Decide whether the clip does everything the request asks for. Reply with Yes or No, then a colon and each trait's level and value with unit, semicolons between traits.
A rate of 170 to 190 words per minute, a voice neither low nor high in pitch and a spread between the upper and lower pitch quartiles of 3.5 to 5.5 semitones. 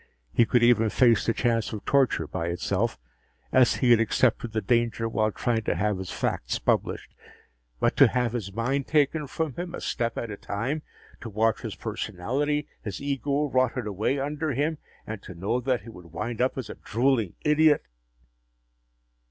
No: average, 180 wpm; low, 120 Hz; average, 4.1 semitones